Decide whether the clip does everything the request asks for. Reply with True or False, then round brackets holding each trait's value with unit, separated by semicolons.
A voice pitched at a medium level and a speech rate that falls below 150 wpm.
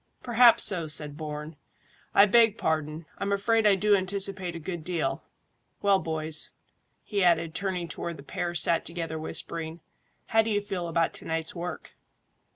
False (175 Hz; 165 wpm)